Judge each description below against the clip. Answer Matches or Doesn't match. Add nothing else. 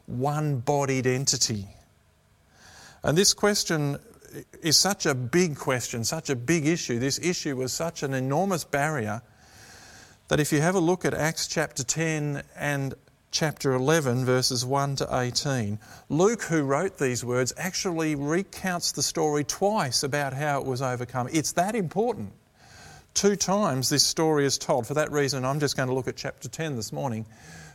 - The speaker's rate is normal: Matches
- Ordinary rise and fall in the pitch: Matches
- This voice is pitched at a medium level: Matches